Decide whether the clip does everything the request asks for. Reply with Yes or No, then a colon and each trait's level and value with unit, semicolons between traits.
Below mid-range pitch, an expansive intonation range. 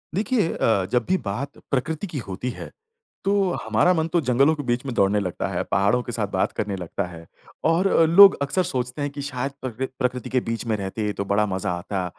Yes: low, 125 Hz; wide, 7.5 semitones